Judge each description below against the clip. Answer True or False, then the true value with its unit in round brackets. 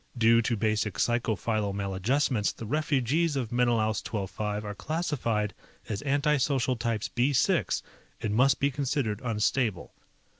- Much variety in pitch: False (4.3 semitones)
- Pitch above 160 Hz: False (115 Hz)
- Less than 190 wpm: True (145 wpm)